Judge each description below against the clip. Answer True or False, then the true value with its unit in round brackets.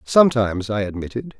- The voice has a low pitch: True (110 Hz)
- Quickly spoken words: False (130 wpm)